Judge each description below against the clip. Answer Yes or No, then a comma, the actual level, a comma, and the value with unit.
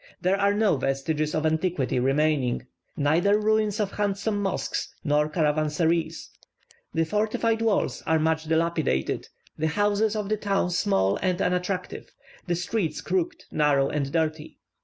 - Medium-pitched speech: Yes, medium, 170 Hz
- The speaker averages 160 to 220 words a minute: No, slow, 135 wpm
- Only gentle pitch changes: No, average, 5.0 semitones